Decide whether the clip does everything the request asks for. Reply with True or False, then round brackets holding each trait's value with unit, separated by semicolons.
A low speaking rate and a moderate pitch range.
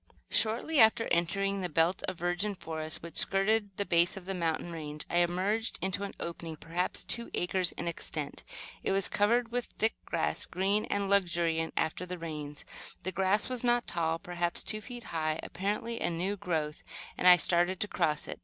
False (185 wpm; 3.3 semitones)